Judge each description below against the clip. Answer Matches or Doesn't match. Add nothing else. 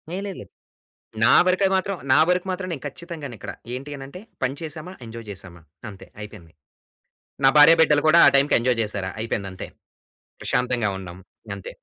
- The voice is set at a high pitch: Doesn't match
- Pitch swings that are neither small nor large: Doesn't match